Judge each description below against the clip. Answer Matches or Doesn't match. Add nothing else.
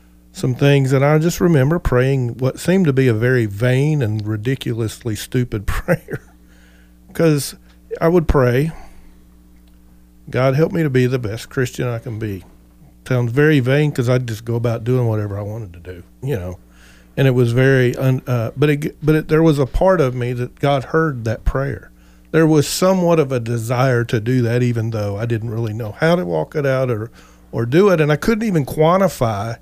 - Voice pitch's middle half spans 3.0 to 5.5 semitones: Matches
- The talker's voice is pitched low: Matches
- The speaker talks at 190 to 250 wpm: Matches